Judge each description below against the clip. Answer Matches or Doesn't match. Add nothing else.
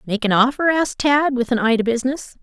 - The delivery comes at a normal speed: Doesn't match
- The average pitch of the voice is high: Matches